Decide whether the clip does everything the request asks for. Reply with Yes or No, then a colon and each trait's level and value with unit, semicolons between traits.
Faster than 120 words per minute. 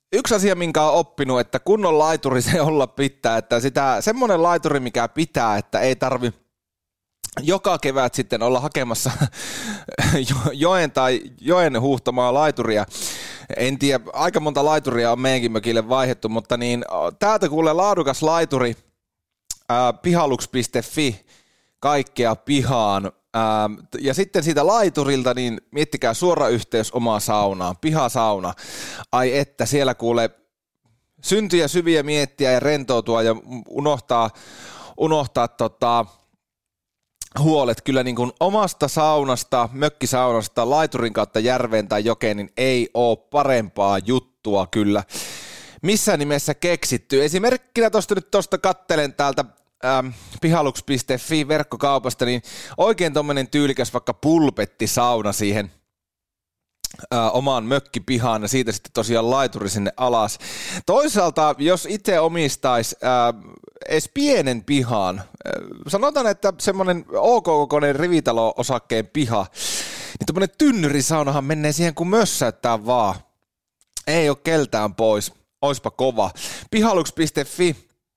No: average, 115 wpm